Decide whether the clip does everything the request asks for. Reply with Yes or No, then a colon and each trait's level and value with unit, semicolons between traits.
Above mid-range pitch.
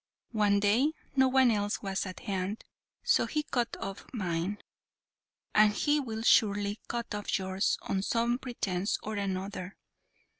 Yes: high, 205 Hz